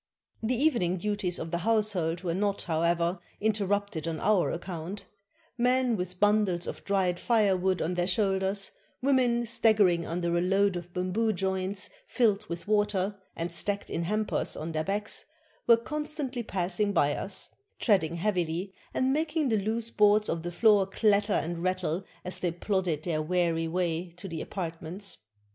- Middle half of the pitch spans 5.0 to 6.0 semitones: No, average, 3.5 semitones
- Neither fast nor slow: Yes, average, 160 wpm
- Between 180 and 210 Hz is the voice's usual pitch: Yes, high, 190 Hz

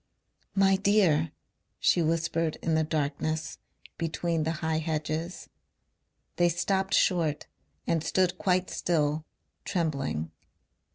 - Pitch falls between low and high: Yes, medium, 165 Hz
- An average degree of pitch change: No, narrow, 2.3 semitones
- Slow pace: Yes, slow, 105 wpm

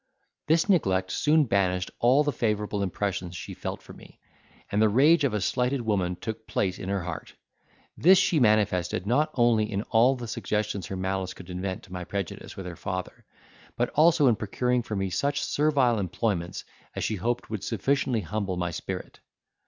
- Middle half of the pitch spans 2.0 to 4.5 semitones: No, average, 5.0 semitones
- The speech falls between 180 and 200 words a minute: Yes, average, 185 wpm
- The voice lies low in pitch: Yes, low, 105 Hz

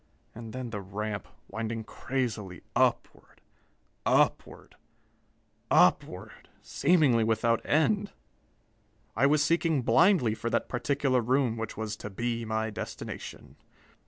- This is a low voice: Yes, low, 115 Hz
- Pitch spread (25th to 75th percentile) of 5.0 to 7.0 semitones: No, average, 4.0 semitones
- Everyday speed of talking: No, slow, 110 wpm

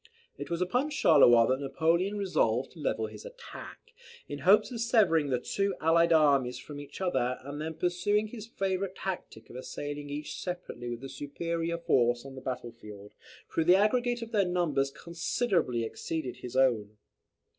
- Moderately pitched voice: Yes, medium, 160 Hz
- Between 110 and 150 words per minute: No, average, 170 wpm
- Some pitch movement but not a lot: No, wide, 6.2 semitones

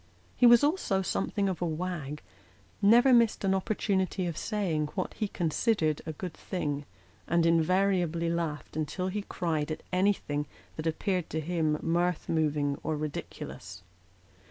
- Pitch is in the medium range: Yes, medium, 170 Hz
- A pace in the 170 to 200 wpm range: No, average, 145 wpm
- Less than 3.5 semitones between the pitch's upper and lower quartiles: No, average, 3.8 semitones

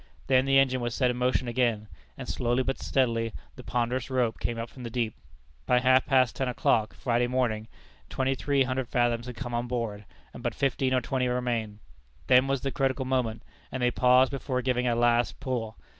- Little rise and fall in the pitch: Yes, narrow, 1.7 semitones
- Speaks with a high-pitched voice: No, low, 125 Hz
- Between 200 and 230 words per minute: Yes, fast, 205 wpm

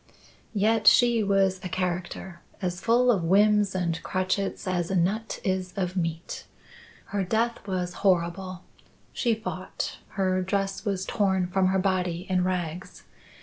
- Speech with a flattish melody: Yes, narrow, 1.8 semitones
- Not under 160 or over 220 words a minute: No, average, 145 wpm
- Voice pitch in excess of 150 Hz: Yes, medium, 185 Hz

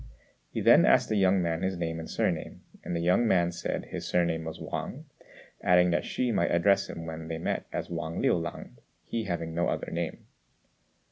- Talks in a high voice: No, very low, 85 Hz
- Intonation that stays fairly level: Yes, narrow, 1.9 semitones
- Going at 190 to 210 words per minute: Yes, average, 200 wpm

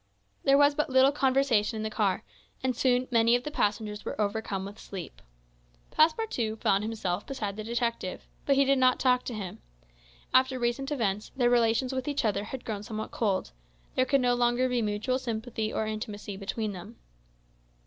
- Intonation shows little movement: No, average, 3.5 semitones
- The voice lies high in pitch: Yes, high, 235 Hz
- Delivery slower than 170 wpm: No, average, 180 wpm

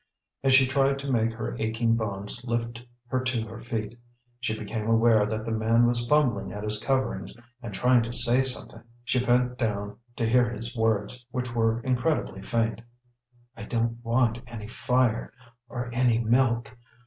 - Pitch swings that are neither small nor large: No, narrow, 1.9 semitones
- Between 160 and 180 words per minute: Yes, average, 170 wpm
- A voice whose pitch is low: Yes, low, 115 Hz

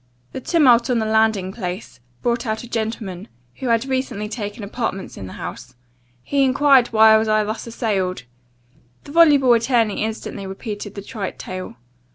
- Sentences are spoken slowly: No, average, 165 wpm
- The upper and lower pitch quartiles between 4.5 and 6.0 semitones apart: No, average, 3.3 semitones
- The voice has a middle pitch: No, high, 220 Hz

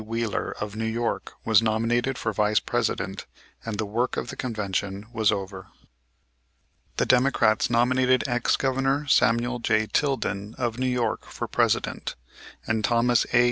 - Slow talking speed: No, average, 145 wpm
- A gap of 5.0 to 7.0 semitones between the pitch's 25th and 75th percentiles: No, narrow, 2.6 semitones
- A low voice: Yes, low, 115 Hz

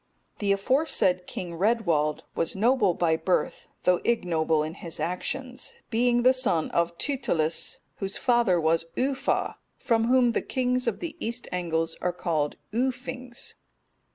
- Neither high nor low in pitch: No, high, 200 Hz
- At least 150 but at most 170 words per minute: No, average, 140 wpm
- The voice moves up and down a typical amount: No, wide, 6.7 semitones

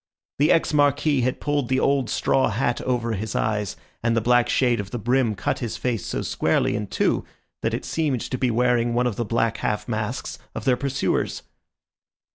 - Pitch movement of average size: Yes, average, 3.0 semitones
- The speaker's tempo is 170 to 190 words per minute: No, average, 200 wpm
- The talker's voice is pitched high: No, low, 120 Hz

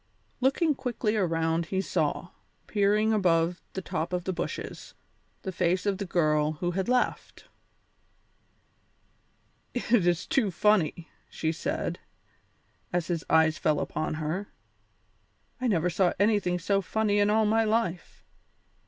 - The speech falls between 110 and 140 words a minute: Yes, slow, 135 wpm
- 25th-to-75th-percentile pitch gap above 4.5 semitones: No, average, 4.1 semitones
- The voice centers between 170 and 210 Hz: Yes, medium, 185 Hz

